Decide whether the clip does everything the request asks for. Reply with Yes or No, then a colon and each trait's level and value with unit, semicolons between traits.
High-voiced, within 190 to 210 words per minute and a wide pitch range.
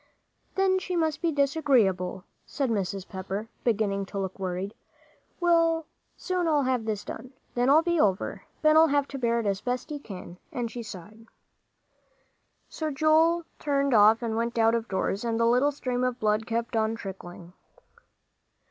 No: high, 235 Hz; average, 165 wpm; wide, 6.0 semitones